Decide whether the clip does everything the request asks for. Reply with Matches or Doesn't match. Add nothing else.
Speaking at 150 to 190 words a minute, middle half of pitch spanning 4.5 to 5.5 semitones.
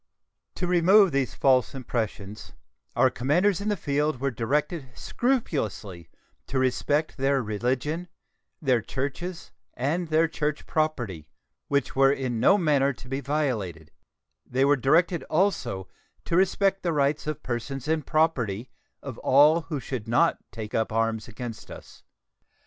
Doesn't match